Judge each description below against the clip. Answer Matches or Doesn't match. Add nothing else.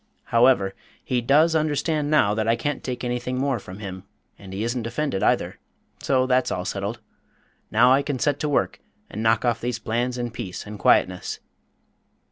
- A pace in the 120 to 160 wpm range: Doesn't match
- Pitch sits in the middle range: Doesn't match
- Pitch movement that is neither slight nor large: Matches